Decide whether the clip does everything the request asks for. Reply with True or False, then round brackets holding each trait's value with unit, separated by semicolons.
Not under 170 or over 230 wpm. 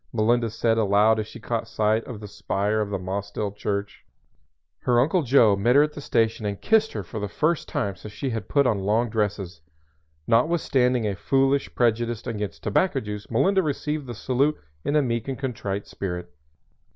True (190 wpm)